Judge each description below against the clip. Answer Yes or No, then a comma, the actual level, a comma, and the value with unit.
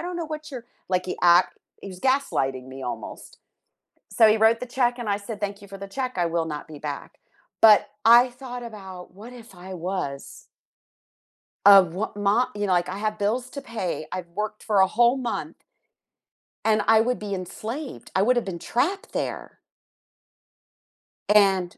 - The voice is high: Yes, high, 210 Hz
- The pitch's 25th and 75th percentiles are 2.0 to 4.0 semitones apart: No, average, 4.7 semitones